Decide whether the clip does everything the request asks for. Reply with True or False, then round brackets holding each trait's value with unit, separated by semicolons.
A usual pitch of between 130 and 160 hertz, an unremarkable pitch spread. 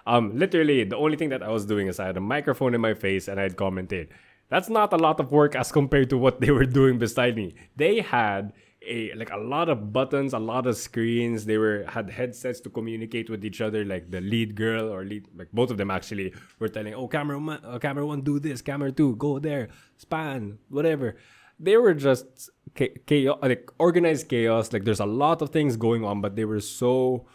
False (120 Hz; 4.6 semitones)